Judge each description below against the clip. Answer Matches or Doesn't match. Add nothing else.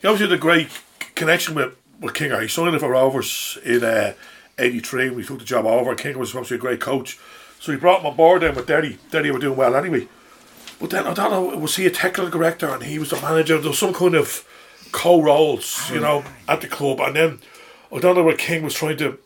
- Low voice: Doesn't match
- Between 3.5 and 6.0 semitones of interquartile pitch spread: Matches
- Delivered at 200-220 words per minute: Doesn't match